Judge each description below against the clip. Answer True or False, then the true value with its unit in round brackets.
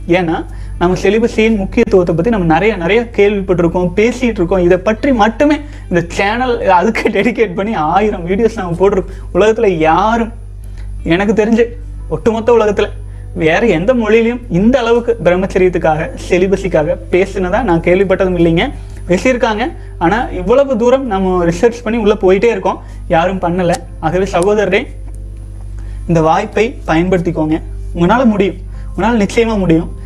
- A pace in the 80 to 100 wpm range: False (125 wpm)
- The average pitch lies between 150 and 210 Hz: True (190 Hz)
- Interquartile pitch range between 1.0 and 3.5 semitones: False (4.8 semitones)